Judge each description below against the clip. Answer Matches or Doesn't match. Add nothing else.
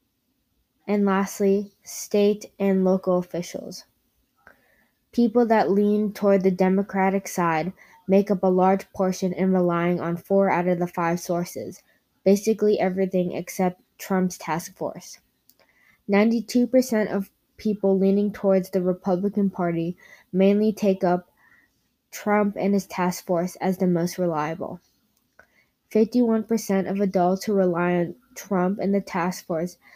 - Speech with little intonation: Matches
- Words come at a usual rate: Doesn't match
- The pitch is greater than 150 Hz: Matches